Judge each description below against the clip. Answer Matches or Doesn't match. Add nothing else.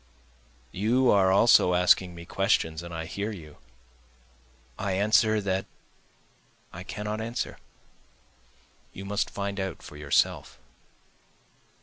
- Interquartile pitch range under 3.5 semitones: Matches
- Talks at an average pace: Doesn't match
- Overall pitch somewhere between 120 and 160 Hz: Doesn't match